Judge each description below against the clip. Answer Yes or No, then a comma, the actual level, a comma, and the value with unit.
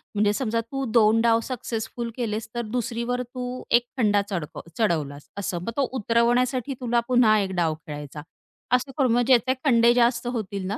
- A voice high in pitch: Yes, high, 235 Hz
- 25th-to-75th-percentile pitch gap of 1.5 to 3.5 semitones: Yes, average, 3.1 semitones